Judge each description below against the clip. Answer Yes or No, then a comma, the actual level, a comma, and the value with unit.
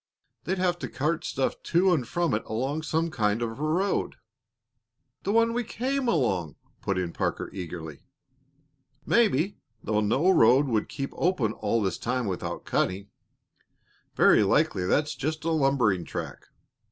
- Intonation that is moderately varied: No, wide, 8.4 semitones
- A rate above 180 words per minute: No, average, 155 wpm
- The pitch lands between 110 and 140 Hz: Yes, low, 135 Hz